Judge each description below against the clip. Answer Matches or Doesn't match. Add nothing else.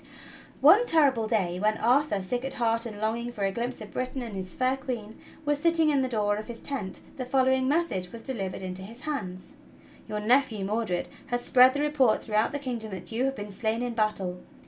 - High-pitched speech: Matches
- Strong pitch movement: Doesn't match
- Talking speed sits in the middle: Doesn't match